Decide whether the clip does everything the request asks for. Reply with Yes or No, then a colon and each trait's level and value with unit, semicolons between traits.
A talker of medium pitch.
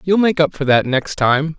Yes: medium, 155 Hz